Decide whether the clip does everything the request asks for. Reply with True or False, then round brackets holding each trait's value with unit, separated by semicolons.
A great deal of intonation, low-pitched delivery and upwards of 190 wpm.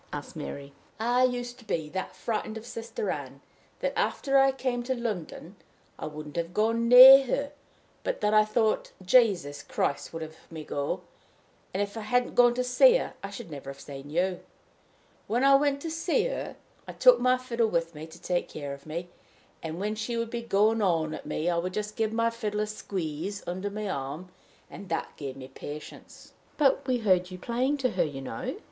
False (6.9 semitones; 210 Hz; 205 wpm)